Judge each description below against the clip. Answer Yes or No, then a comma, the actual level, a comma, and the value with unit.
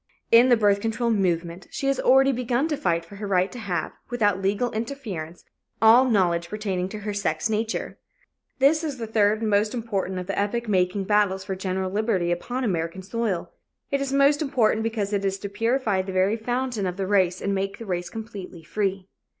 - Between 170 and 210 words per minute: Yes, average, 200 wpm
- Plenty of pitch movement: No, average, 3.7 semitones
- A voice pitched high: Yes, high, 205 Hz